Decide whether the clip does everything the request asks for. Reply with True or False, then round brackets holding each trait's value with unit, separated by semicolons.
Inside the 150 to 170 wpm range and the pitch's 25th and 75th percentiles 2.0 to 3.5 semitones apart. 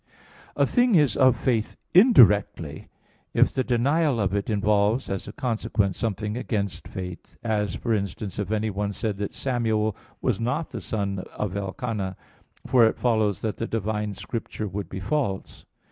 True (160 wpm; 3.0 semitones)